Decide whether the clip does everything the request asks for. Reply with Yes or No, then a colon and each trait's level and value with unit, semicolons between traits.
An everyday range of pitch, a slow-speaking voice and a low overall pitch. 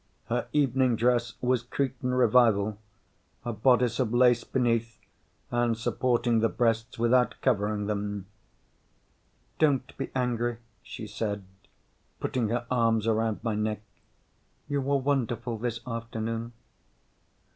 No: narrow, 2.0 semitones; slow, 115 wpm; low, 115 Hz